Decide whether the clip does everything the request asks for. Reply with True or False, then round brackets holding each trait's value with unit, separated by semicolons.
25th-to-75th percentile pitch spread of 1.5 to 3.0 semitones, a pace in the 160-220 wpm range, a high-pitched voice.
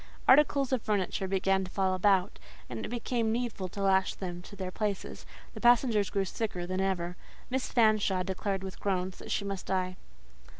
True (2.6 semitones; 180 wpm; 195 Hz)